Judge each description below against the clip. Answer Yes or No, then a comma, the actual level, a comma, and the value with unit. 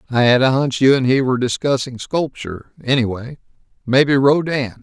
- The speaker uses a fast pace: No, average, 160 wpm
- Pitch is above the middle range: No, low, 130 Hz